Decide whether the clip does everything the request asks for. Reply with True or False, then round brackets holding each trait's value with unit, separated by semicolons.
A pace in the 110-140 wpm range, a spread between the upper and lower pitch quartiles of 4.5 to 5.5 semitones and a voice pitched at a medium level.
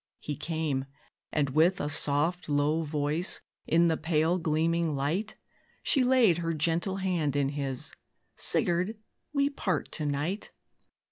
False (135 wpm; 3.4 semitones; 160 Hz)